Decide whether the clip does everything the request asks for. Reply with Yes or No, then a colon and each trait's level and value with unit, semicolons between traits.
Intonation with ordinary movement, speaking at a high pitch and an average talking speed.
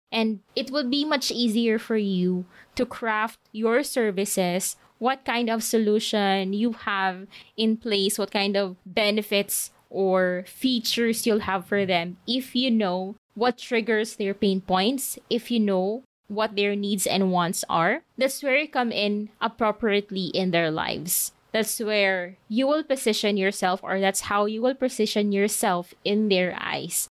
Yes: average, 3.2 semitones; high, 210 Hz; average, 160 wpm